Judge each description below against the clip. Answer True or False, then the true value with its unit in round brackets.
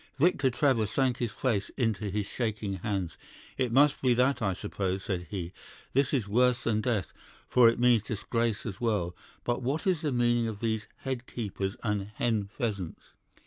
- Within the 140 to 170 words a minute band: False (180 wpm)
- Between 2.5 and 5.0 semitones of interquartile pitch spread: True (3.6 semitones)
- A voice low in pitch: True (115 Hz)